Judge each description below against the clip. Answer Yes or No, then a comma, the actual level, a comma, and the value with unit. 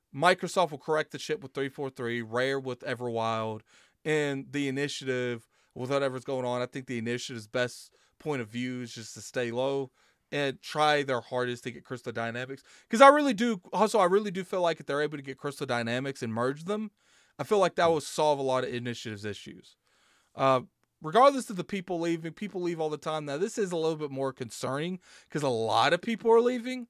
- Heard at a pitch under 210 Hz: Yes, medium, 140 Hz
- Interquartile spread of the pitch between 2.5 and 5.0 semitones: No, wide, 5.6 semitones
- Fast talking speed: Yes, fast, 210 wpm